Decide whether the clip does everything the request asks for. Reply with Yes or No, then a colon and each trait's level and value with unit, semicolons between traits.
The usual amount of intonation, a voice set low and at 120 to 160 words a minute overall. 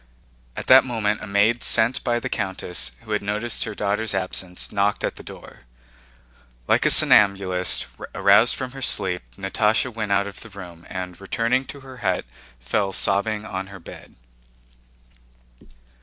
Yes: average, 3.0 semitones; low, 100 Hz; average, 155 wpm